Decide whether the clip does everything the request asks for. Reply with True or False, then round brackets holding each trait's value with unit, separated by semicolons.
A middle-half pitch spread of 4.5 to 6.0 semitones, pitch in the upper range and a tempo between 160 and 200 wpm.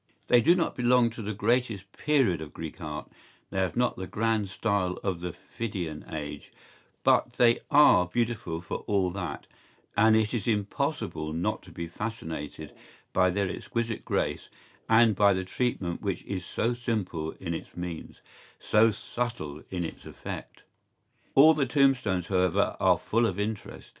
False (4.8 semitones; 100 Hz; 165 wpm)